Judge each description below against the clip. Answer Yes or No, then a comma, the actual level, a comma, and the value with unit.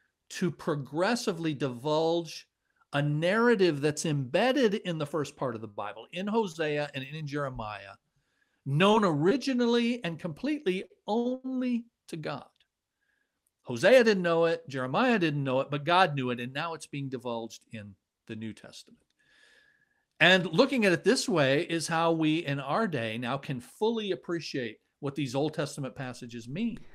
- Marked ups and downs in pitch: Yes, wide, 6.8 semitones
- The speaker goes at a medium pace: Yes, average, 155 wpm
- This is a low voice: No, medium, 165 Hz